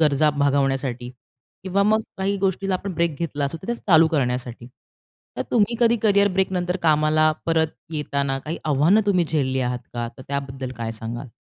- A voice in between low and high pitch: Yes, medium, 155 Hz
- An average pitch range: No, wide, 5.8 semitones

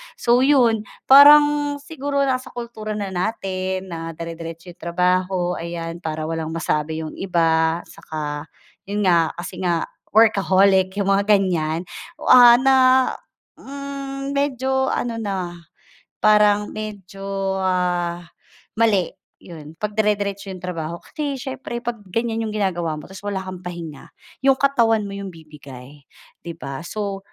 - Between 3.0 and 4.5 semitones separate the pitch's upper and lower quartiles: No, average, 5.1 semitones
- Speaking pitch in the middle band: No, high, 195 Hz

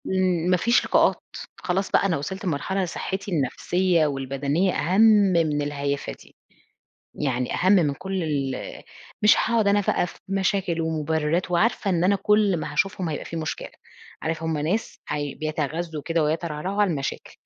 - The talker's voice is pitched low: No, medium, 170 Hz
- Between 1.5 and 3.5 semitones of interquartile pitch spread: No, average, 4.2 semitones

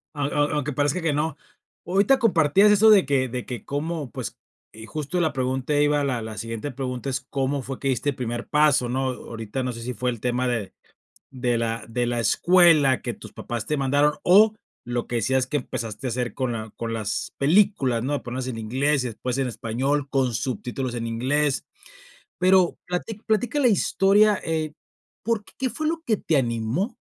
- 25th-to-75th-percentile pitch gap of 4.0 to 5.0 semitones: Yes, average, 4.7 semitones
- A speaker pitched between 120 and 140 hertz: Yes, low, 135 Hz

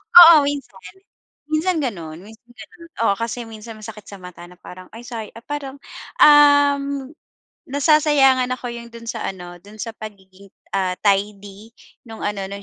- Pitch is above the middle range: Yes, high, 225 Hz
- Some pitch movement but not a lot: No, wide, 5.9 semitones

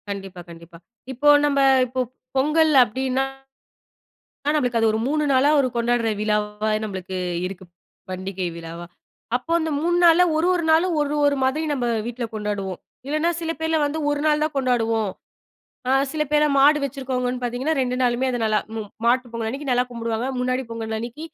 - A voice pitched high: Yes, very high, 250 Hz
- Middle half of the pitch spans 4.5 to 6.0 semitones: Yes, average, 4.9 semitones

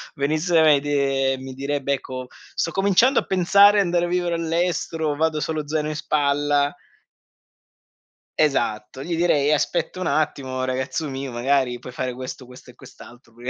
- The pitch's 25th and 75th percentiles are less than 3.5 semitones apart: No, average, 3.9 semitones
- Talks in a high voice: No, medium, 145 Hz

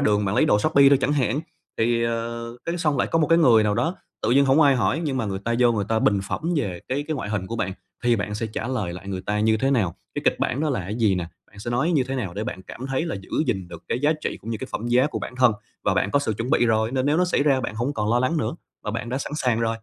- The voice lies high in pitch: No, low, 120 Hz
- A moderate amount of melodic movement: Yes, average, 4.6 semitones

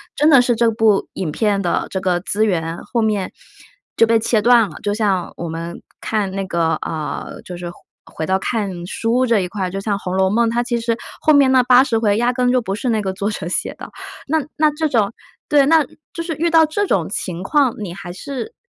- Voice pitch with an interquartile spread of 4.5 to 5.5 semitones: Yes, average, 4.8 semitones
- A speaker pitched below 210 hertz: No, high, 220 Hz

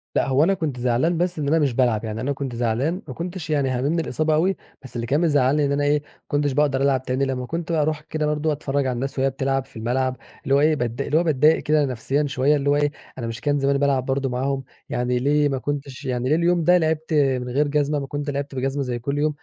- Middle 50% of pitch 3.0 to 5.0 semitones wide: No, narrow, 2.6 semitones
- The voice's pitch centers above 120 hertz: Yes, medium, 140 Hz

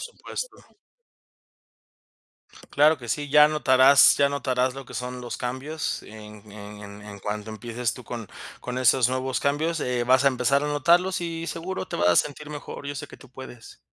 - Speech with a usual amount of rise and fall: Yes, average, 3.7 semitones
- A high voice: No, low, 130 Hz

